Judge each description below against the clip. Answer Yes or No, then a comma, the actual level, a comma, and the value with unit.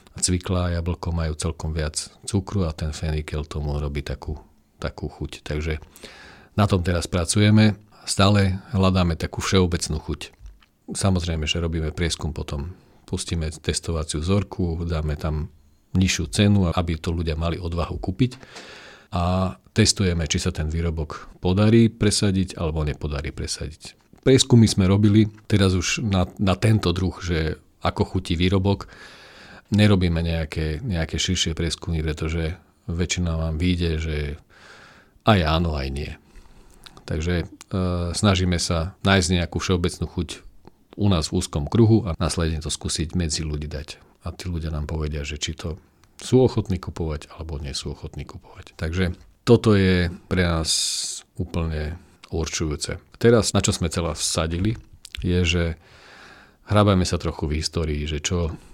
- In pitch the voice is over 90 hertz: No, very low, 85 Hz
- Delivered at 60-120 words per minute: No, average, 140 wpm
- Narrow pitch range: No, average, 3.3 semitones